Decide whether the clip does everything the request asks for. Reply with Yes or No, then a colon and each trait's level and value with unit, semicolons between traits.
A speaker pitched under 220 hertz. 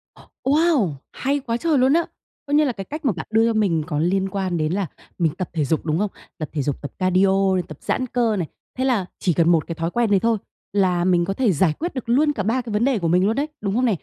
Yes: high, 200 Hz